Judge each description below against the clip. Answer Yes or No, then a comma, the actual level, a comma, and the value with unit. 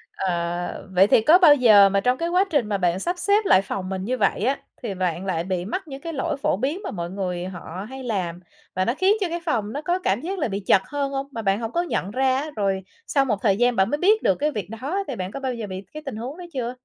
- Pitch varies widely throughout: Yes, wide, 7.2 semitones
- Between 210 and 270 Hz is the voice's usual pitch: Yes, high, 230 Hz